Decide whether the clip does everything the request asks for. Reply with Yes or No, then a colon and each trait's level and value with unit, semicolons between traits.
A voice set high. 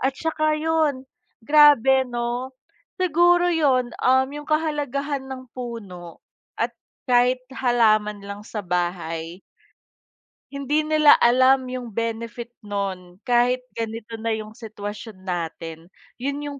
Yes: high, 245 Hz